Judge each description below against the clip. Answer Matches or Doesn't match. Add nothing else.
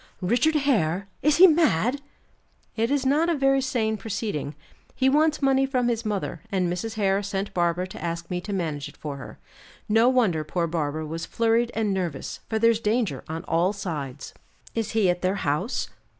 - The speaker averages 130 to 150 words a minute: Doesn't match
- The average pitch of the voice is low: Doesn't match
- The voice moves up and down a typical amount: Doesn't match